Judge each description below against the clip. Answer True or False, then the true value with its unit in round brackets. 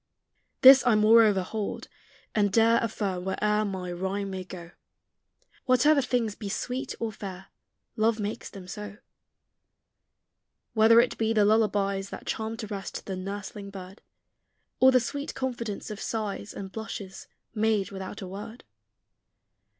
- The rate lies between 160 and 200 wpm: False (140 wpm)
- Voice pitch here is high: True (210 Hz)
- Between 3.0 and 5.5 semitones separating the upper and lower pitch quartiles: False (2.6 semitones)